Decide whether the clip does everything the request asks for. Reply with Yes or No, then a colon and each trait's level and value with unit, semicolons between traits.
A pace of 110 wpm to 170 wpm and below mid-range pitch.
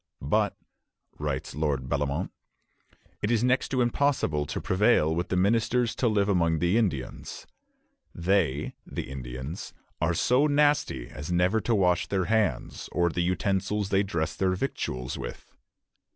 Yes: average, 145 wpm; very low, 90 Hz